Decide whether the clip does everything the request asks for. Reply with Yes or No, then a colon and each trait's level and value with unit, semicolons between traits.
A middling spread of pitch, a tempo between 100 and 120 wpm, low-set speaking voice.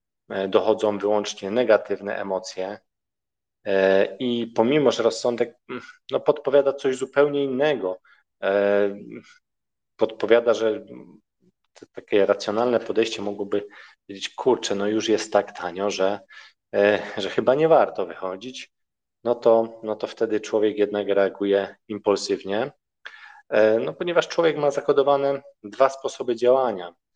Yes: average, 3.8 semitones; slow, 110 wpm; low, 105 Hz